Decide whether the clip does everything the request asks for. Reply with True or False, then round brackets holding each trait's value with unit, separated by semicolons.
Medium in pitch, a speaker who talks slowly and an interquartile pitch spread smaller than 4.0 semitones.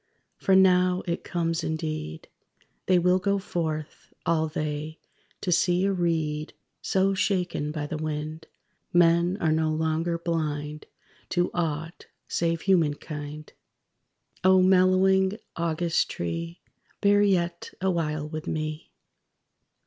True (165 Hz; 120 wpm; 2.9 semitones)